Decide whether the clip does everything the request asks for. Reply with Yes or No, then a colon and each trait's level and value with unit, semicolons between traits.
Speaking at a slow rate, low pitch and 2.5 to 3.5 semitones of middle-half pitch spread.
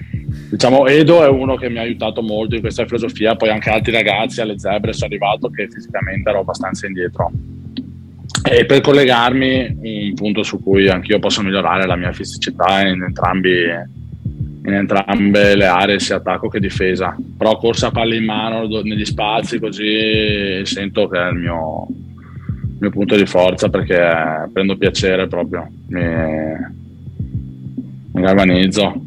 No: average, 155 wpm; low, 105 Hz; average, 3.2 semitones